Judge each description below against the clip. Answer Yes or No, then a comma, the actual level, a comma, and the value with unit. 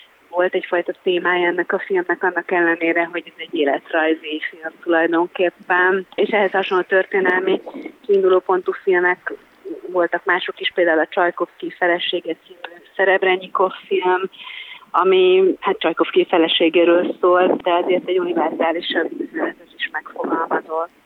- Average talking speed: Yes, average, 120 wpm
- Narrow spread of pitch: Yes, narrow, 2.1 semitones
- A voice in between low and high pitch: Yes, medium, 180 Hz